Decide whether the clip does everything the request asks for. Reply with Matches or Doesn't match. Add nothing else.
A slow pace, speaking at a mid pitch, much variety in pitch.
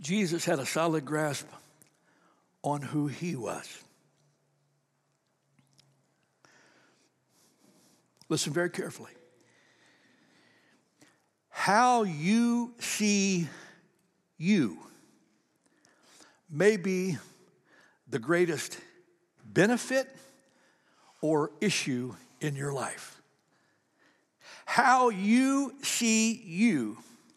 Matches